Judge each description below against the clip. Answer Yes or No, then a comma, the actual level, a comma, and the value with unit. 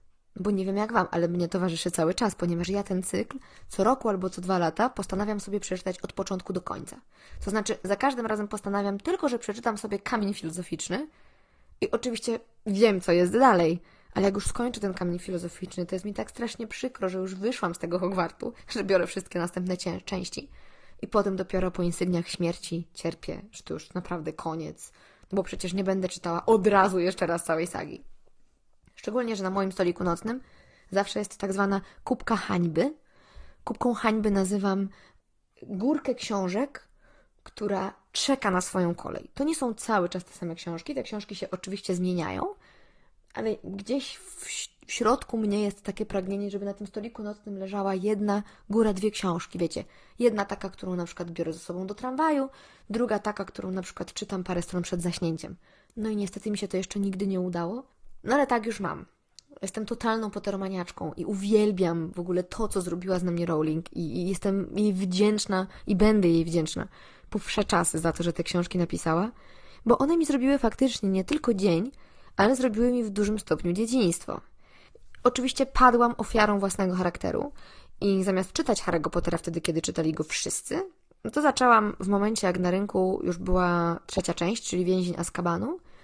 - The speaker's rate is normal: No, fast, 180 wpm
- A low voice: No, high, 195 Hz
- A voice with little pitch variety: No, average, 3.4 semitones